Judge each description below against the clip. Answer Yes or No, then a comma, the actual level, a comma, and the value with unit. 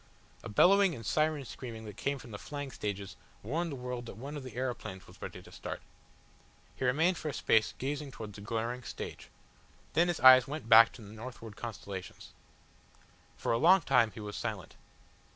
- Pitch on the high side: No, low, 125 Hz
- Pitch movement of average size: Yes, average, 4.7 semitones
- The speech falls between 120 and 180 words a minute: No, average, 190 wpm